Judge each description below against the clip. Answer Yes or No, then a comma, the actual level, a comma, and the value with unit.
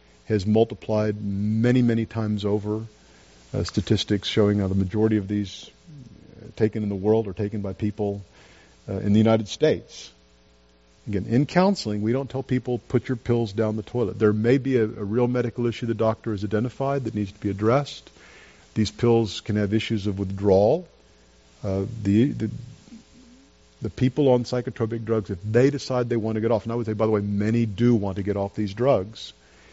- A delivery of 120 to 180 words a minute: No, average, 190 wpm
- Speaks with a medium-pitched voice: No, low, 110 Hz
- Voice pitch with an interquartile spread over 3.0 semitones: No, average, 2.7 semitones